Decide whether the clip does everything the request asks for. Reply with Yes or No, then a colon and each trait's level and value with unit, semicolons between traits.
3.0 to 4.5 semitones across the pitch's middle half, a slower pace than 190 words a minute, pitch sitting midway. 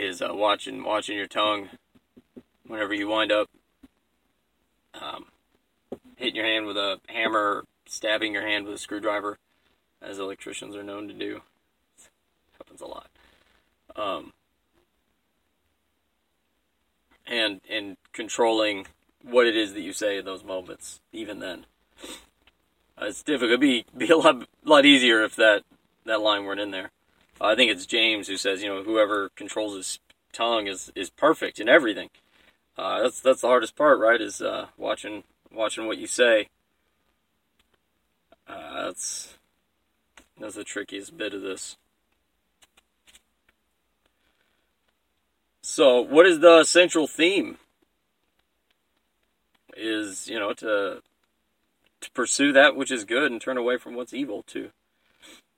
No: average, 3.4 semitones; average, 140 wpm; low, 105 Hz